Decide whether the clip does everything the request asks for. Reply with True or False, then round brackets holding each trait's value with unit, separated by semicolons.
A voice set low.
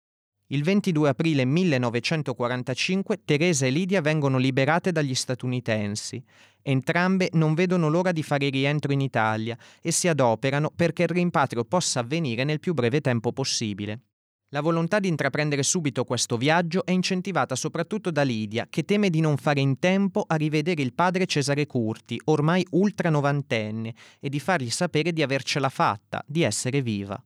False (145 Hz)